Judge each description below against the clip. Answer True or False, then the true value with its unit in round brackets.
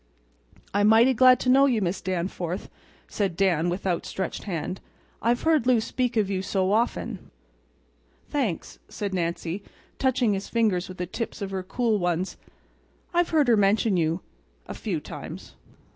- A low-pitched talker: False (200 Hz)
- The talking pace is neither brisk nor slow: True (155 wpm)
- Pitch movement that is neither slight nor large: True (4.7 semitones)